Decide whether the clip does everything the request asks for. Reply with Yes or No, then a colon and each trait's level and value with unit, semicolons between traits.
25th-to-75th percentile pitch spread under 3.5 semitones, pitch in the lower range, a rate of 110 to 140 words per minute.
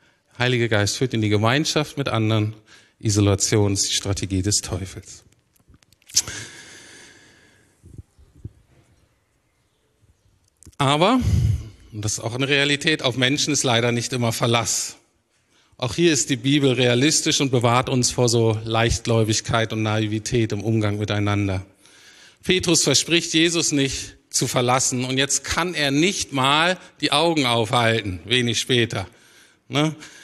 No: average, 4.4 semitones; low, 115 Hz; slow, 125 wpm